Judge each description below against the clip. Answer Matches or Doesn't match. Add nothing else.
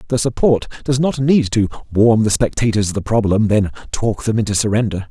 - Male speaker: Matches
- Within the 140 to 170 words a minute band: Doesn't match